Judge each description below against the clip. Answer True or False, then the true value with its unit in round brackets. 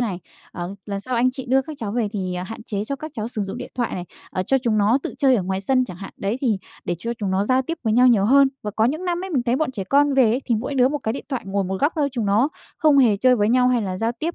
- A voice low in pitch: False (240 Hz)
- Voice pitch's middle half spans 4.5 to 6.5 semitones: True (4.8 semitones)